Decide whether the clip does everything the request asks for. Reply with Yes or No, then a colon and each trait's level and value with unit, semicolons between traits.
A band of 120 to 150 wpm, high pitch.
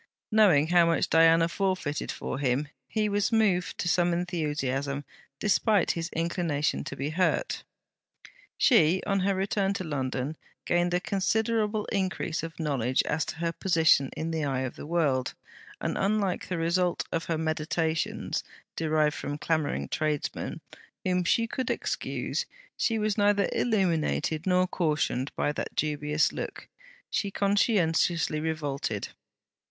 No: average, 140 wpm; medium, 165 Hz